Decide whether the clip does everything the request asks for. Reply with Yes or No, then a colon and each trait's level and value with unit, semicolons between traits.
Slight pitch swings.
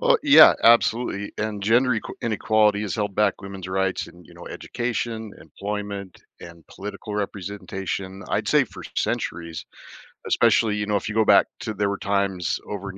Yes: narrow, 2.0 semitones